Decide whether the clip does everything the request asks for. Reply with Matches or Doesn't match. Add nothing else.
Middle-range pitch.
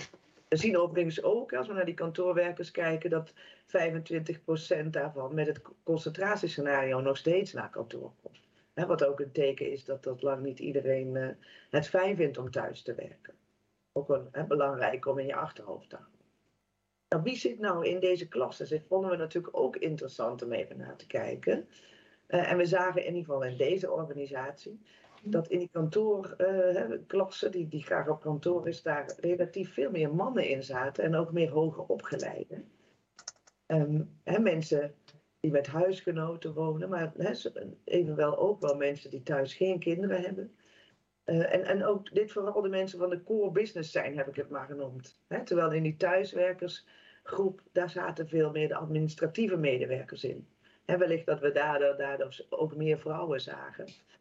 Matches